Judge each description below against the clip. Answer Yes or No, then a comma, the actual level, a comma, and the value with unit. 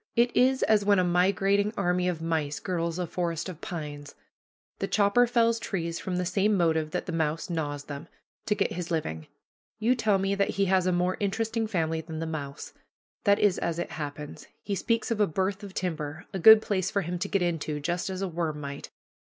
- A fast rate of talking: Yes, fast, 215 wpm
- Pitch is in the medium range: Yes, medium, 180 Hz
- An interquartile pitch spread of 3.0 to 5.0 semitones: Yes, average, 3.8 semitones